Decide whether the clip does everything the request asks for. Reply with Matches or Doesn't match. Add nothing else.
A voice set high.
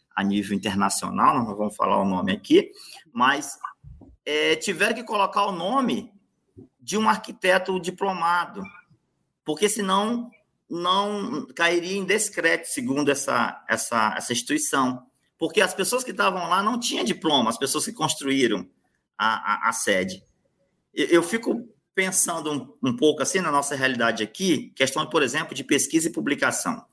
Doesn't match